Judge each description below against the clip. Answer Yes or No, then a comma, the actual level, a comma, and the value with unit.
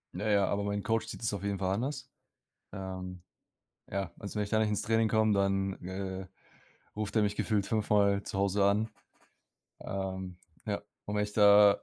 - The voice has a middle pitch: No, low, 100 Hz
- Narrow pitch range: Yes, narrow, 1.4 semitones